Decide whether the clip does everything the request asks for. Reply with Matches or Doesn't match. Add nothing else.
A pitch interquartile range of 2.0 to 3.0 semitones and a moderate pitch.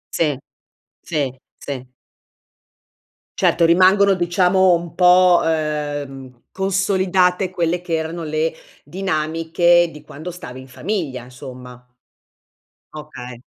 Doesn't match